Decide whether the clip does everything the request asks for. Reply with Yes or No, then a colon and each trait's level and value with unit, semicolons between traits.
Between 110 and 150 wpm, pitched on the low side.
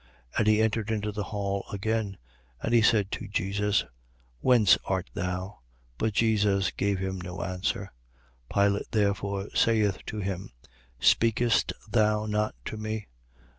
Yes: average, 145 wpm; low, 105 Hz